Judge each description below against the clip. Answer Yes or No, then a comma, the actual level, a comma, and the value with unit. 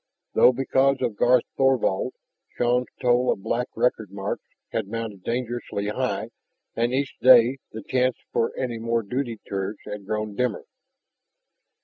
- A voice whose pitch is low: Yes, low, 120 Hz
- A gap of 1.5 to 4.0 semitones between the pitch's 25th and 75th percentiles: Yes, average, 2.9 semitones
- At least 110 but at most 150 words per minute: Yes, average, 140 wpm